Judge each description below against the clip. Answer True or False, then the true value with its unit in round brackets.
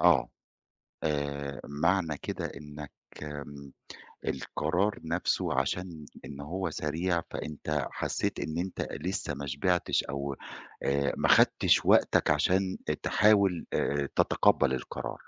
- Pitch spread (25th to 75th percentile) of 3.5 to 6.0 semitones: True (4.0 semitones)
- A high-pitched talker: False (75 Hz)